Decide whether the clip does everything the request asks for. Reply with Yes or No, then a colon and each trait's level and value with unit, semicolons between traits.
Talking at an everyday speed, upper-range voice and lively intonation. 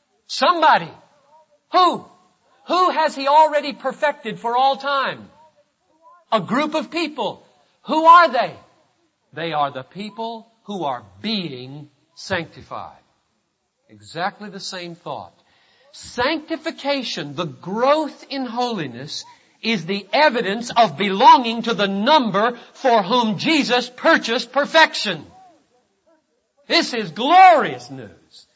No: slow, 105 wpm; very high, 250 Hz; wide, 7.6 semitones